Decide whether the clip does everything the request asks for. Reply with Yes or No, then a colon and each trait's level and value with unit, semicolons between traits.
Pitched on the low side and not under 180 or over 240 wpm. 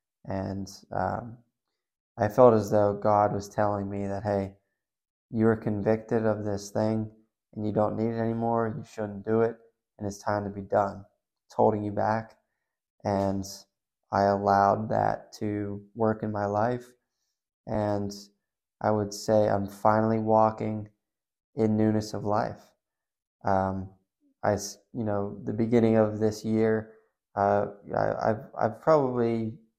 No: low, 105 Hz; average, 145 wpm